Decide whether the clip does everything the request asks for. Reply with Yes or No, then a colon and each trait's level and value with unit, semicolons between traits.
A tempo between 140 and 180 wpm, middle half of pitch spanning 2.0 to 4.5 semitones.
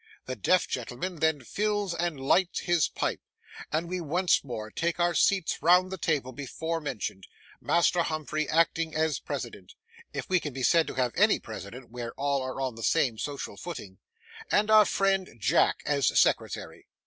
No: average, 165 wpm; wide, 5.5 semitones